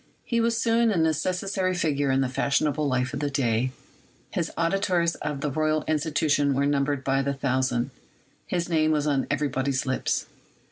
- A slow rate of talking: No, average, 170 wpm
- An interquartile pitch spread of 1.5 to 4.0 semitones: Yes, average, 3.5 semitones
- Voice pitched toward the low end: No, medium, 145 Hz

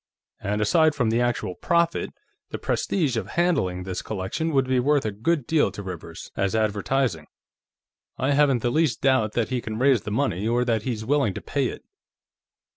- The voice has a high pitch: No, low, 120 Hz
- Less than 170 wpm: No, average, 190 wpm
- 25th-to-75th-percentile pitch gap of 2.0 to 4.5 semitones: No, average, 5.2 semitones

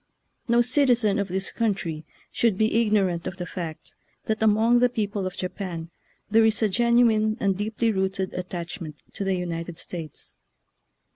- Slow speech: No, average, 165 wpm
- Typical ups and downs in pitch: Yes, average, 3.6 semitones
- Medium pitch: No, high, 200 Hz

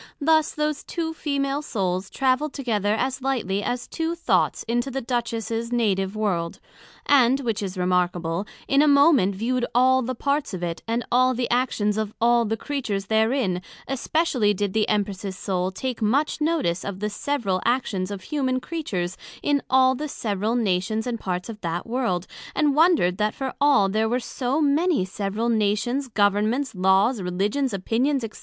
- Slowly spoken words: No, average, 170 wpm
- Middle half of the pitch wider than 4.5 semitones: Yes, wide, 5.4 semitones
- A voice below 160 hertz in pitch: No, high, 230 Hz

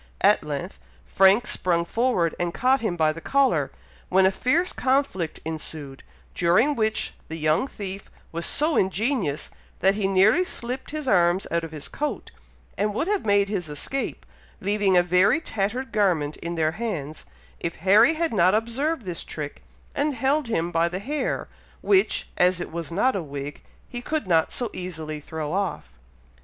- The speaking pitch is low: No, high, 190 Hz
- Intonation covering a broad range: Yes, wide, 6.6 semitones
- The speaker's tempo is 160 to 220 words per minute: Yes, average, 170 wpm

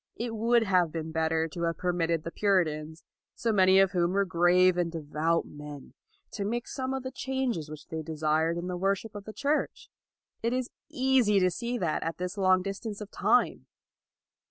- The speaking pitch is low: No, medium, 185 Hz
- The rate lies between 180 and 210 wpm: Yes, average, 195 wpm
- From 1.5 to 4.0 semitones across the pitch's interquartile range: No, average, 4.9 semitones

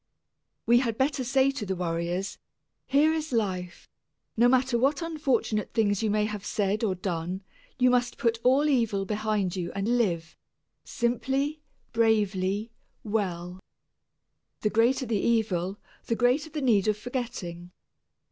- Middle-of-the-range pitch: No, high, 220 Hz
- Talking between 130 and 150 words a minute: Yes, average, 140 wpm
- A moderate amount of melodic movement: Yes, average, 4.5 semitones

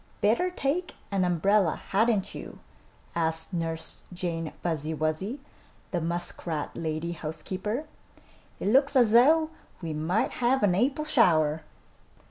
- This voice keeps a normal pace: No, slow, 120 wpm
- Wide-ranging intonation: Yes, wide, 6.7 semitones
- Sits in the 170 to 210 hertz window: Yes, medium, 185 Hz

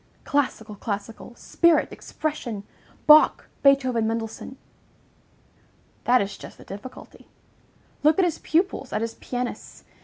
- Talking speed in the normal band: No, slow, 115 wpm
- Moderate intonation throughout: Yes, average, 5.0 semitones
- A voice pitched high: Yes, very high, 250 Hz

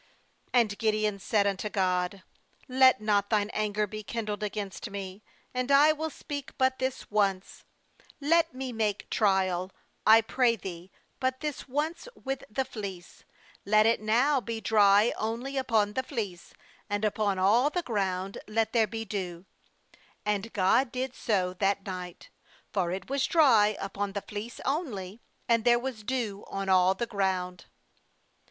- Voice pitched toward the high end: Yes, high, 215 Hz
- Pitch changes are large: No, average, 4.3 semitones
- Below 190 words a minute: Yes, average, 155 wpm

